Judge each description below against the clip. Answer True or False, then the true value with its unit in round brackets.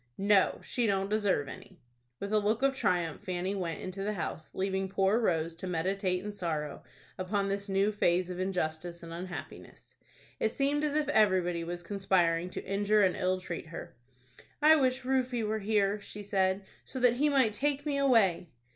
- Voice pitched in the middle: False (195 Hz)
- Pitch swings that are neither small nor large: True (3.2 semitones)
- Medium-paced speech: True (180 wpm)